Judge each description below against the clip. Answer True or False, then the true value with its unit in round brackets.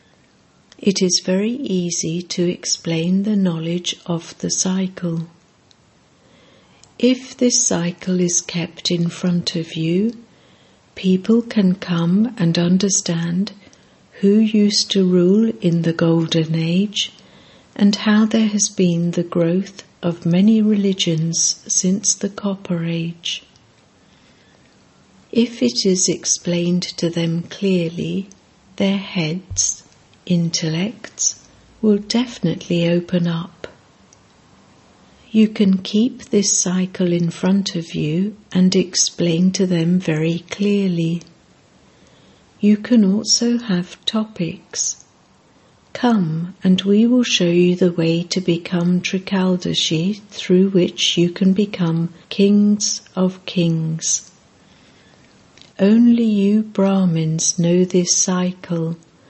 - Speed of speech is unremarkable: False (105 wpm)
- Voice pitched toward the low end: False (185 Hz)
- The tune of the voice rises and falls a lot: False (3.0 semitones)